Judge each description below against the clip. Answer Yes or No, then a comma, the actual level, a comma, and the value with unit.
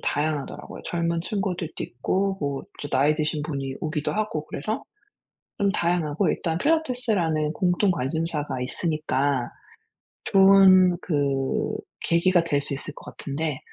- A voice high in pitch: No, medium, 160 Hz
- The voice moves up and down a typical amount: Yes, average, 4.4 semitones